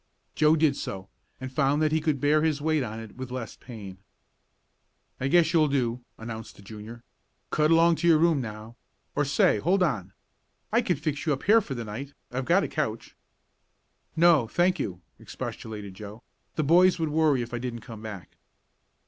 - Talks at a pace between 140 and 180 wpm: No, average, 190 wpm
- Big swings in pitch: Yes, wide, 5.8 semitones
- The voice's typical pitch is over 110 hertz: Yes, low, 135 Hz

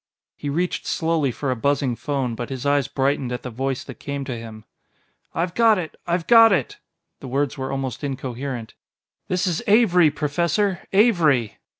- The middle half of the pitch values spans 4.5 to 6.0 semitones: Yes, average, 4.9 semitones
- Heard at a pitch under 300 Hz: Yes, medium, 140 Hz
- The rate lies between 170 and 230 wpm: Yes, average, 175 wpm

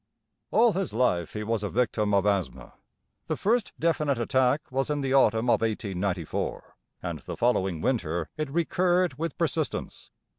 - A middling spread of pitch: No, wide, 6.8 semitones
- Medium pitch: No, low, 125 Hz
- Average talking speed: Yes, average, 155 wpm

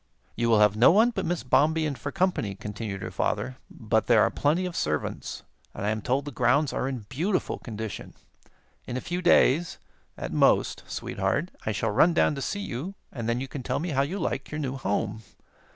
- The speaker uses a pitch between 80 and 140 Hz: Yes, low, 135 Hz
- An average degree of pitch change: No, wide, 6.6 semitones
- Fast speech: Yes, fast, 210 wpm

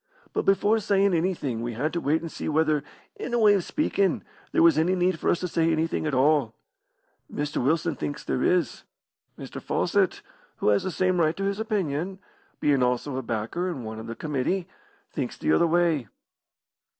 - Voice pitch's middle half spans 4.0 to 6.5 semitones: Yes, average, 4.6 semitones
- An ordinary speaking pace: Yes, average, 195 wpm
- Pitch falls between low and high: Yes, medium, 160 Hz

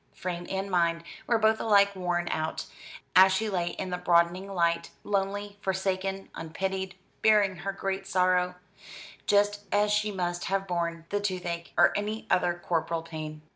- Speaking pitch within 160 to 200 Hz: Yes, high, 190 Hz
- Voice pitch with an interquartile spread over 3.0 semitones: No, narrow, 2.4 semitones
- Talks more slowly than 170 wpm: Yes, average, 155 wpm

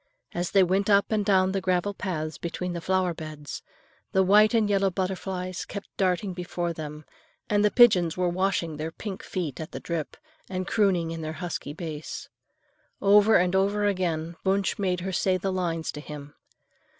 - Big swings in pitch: No, average, 2.9 semitones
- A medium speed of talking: Yes, average, 175 wpm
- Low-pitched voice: No, medium, 185 Hz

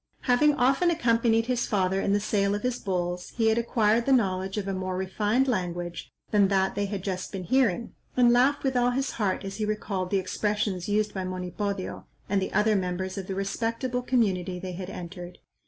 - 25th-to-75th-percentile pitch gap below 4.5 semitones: Yes, average, 3.8 semitones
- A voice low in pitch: No, high, 205 Hz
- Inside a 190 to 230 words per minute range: Yes, fast, 205 wpm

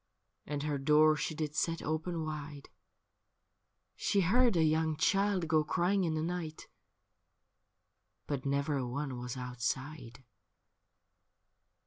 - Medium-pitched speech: Yes, medium, 155 Hz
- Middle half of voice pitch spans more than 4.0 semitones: No, average, 2.7 semitones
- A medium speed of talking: No, slow, 120 wpm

